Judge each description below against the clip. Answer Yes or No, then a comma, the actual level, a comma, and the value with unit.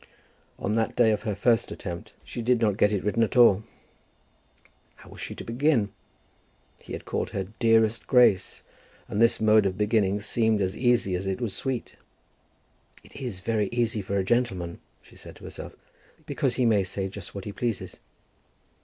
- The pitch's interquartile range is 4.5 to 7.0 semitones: No, average, 3.1 semitones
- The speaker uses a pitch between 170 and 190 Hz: No, low, 110 Hz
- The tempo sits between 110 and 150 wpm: No, average, 180 wpm